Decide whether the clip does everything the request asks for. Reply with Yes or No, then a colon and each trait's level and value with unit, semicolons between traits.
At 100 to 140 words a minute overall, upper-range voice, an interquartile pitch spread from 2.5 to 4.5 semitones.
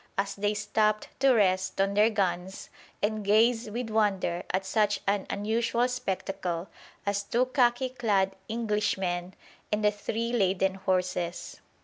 Yes: slow, 135 wpm; high, 205 Hz; average, 2.8 semitones